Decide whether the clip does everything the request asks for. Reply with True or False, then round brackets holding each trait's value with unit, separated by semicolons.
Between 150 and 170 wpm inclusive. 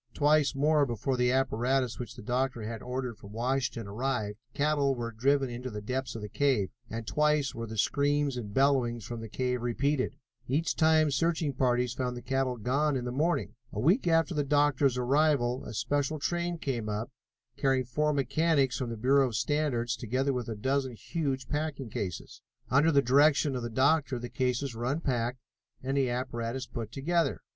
False (185 wpm)